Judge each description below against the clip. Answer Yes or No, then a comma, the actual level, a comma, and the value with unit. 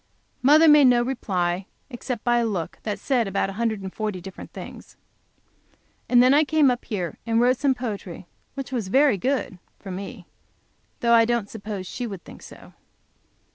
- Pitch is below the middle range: No, high, 230 Hz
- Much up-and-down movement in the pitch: No, average, 4.5 semitones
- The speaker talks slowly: No, average, 180 wpm